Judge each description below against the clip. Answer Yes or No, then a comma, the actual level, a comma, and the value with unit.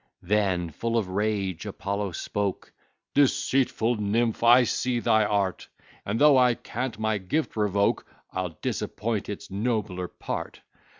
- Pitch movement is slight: No, average, 3.1 semitones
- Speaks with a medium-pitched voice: No, low, 105 Hz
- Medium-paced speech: No, slow, 130 wpm